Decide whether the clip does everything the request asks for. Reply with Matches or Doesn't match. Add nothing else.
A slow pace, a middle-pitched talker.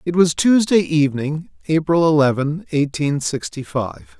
Matches